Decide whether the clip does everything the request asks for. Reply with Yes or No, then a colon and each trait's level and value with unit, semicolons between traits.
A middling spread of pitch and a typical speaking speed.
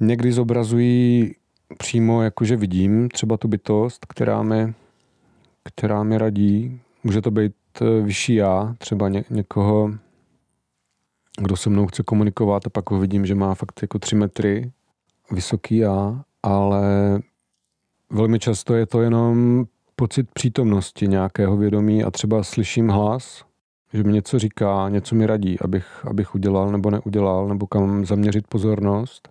No: narrow, 2.3 semitones; average, 140 wpm